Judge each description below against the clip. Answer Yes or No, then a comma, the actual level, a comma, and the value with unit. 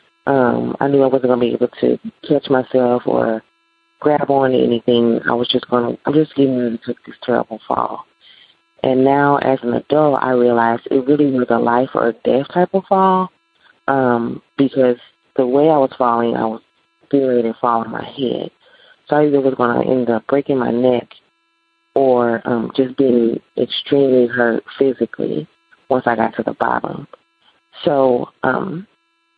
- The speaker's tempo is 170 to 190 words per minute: Yes, average, 180 wpm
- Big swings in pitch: No, average, 3.6 semitones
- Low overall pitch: Yes, low, 130 Hz